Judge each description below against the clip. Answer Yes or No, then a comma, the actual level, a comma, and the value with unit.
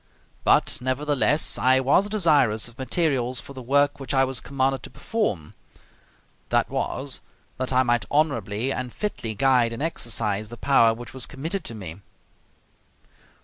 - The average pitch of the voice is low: Yes, low, 130 Hz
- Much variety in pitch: No, average, 3.4 semitones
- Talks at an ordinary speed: Yes, average, 150 wpm